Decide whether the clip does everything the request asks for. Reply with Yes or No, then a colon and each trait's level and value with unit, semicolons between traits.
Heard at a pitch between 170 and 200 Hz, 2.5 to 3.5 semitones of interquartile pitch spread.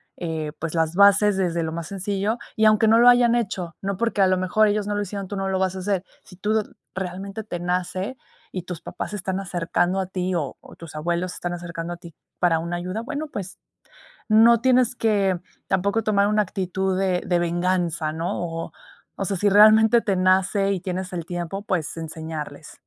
Yes: medium, 185 Hz; average, 2.9 semitones